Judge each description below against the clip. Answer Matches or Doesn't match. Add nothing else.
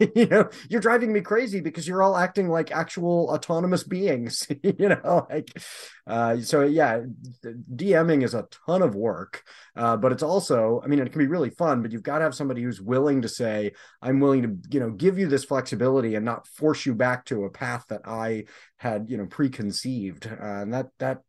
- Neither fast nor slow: Doesn't match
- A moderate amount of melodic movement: Doesn't match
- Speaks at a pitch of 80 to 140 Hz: Matches